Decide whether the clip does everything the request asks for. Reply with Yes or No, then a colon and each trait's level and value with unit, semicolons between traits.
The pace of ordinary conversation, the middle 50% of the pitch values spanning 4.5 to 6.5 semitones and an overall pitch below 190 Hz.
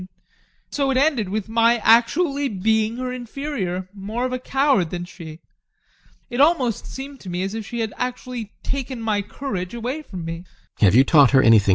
No: average, 165 wpm; average, 5.3 semitones; high, 230 Hz